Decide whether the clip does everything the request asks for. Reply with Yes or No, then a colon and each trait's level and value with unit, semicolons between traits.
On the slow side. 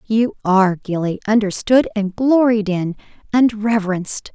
Yes: slow, 125 wpm